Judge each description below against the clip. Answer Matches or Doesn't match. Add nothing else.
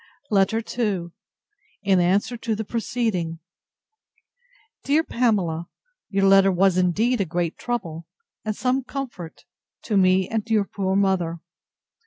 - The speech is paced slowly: Matches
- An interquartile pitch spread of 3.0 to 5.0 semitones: Matches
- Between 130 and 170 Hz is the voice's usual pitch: Doesn't match